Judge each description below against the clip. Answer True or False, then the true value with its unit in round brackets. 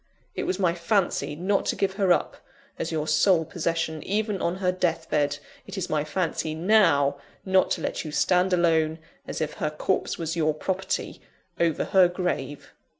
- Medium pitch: True (170 Hz)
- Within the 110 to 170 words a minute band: False (180 wpm)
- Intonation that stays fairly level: False (3.3 semitones)